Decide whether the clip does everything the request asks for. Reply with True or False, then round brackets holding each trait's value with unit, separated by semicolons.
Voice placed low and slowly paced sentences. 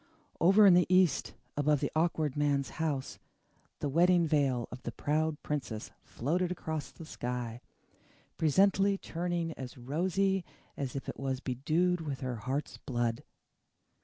False (150 Hz; 130 wpm)